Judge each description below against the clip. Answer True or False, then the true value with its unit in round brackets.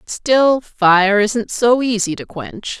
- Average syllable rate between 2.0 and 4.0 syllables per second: True (3.0 syllables/s)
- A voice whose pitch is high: True (215 Hz)